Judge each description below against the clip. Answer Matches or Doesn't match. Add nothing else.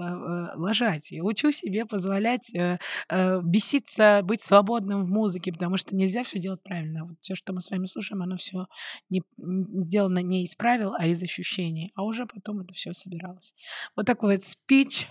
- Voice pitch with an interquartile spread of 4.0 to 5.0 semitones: Doesn't match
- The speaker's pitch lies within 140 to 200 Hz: Matches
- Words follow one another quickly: Matches